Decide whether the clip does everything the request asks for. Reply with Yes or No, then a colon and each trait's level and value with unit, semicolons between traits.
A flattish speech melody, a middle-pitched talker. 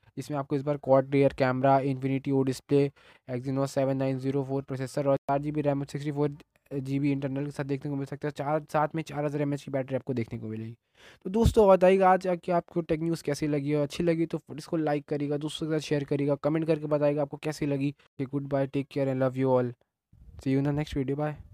Yes: narrow, 1.7 semitones; medium, 145 Hz